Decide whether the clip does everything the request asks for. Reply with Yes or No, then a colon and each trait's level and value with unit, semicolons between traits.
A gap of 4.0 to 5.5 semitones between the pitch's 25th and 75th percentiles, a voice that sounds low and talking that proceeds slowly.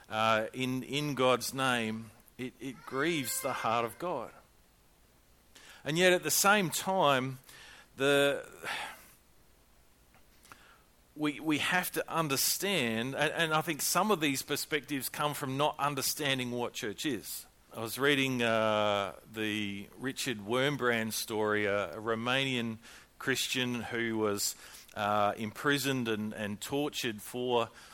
Yes: average, 4.6 semitones; low, 125 Hz; slow, 125 wpm